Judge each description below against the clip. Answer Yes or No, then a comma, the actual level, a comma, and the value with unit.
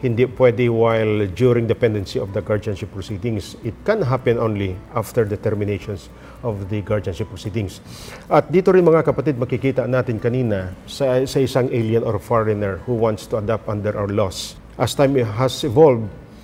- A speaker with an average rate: No, fast, 165 wpm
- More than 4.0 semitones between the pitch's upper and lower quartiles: No, average, 3.4 semitones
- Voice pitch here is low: Yes, low, 115 Hz